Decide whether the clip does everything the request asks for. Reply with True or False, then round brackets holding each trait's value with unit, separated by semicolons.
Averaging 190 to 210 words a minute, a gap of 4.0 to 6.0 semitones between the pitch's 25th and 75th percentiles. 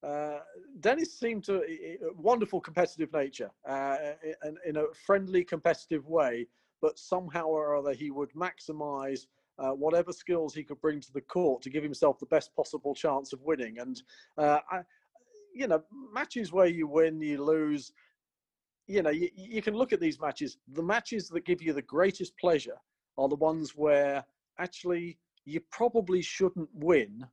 False (170 wpm; 4.4 semitones)